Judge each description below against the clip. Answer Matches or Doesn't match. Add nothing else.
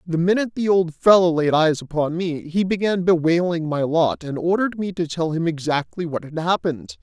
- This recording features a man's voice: Matches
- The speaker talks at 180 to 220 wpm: Matches